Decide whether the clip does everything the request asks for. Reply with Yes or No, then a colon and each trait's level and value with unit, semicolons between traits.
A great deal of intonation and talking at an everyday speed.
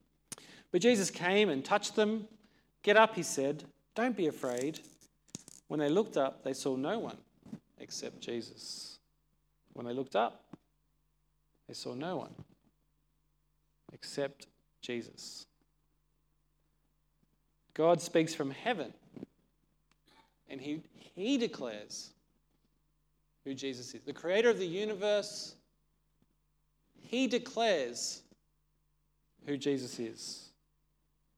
No: wide, 5.8 semitones; slow, 105 wpm